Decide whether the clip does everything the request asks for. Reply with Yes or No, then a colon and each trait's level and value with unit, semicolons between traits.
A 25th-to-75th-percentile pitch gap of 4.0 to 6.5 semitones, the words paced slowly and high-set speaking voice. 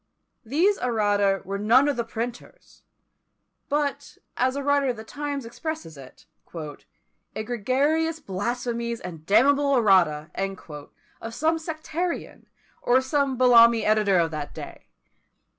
Yes: average, 5.3 semitones; slow, 120 wpm; high, 245 Hz